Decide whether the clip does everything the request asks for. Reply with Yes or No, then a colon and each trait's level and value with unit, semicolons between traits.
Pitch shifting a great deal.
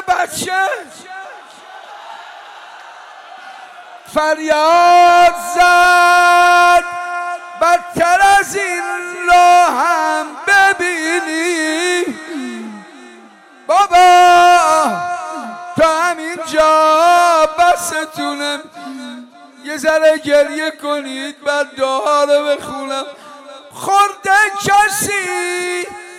No: narrow, 2.5 semitones